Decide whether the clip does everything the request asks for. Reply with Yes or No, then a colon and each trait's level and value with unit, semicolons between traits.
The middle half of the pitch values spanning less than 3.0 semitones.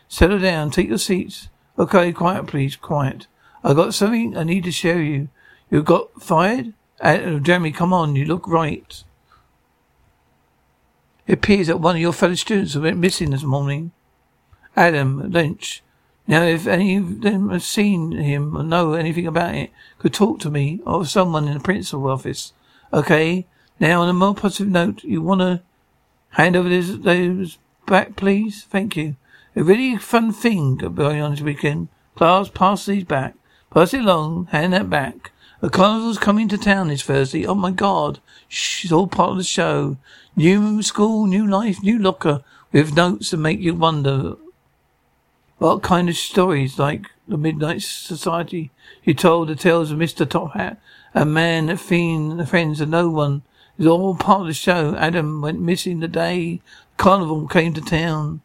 No: average, 3.3 semitones